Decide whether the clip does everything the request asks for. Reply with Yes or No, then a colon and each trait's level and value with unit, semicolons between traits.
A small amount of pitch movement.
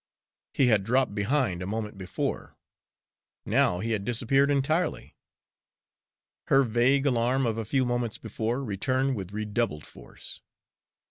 No: average, 4.0 semitones